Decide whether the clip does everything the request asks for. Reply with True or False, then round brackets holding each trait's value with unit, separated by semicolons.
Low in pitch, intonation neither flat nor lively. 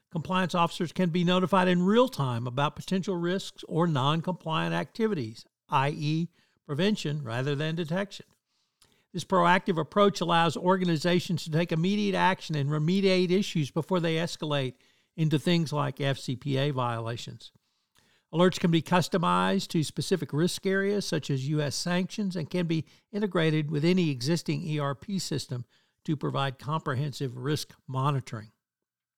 False (165 Hz; 4.0 semitones)